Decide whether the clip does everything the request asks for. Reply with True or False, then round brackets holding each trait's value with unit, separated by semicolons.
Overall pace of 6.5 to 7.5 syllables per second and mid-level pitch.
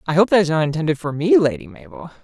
True (7.0 syllables/s; 170 Hz)